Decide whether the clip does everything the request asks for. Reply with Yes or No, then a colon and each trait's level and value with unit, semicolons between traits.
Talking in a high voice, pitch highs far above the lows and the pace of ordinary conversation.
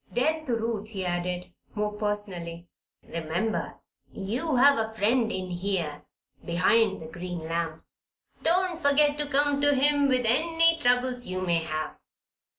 Yes: high, 220 Hz; wide, 7.9 semitones; average, 145 wpm